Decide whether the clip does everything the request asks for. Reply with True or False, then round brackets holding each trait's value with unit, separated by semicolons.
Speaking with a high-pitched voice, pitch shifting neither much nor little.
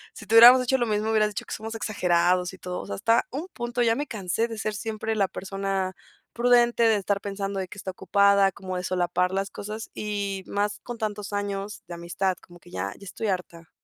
True (200 Hz; 3.0 semitones)